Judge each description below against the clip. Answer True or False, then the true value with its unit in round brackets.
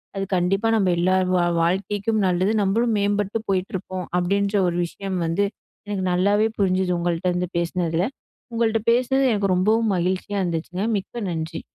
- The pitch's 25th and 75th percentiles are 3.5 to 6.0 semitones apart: False (2.4 semitones)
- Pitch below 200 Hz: True (190 Hz)